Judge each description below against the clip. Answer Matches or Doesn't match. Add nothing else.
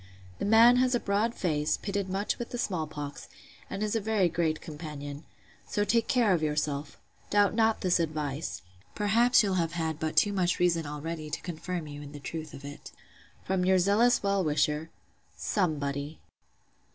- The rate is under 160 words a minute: Doesn't match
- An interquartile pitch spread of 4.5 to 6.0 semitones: Matches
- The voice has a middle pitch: Matches